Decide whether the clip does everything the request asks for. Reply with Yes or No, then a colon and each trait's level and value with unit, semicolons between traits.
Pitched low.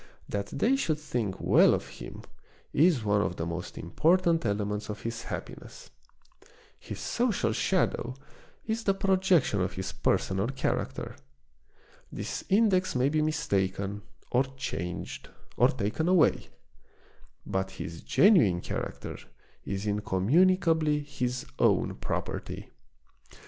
Yes: low, 125 Hz